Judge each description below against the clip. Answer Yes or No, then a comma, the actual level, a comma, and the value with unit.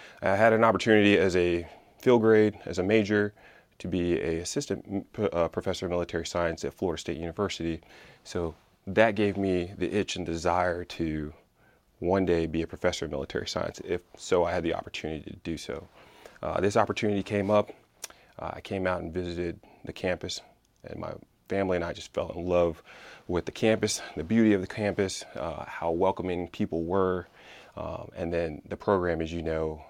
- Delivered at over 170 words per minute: Yes, average, 190 wpm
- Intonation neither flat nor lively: Yes, average, 3.3 semitones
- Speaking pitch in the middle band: No, very low, 90 Hz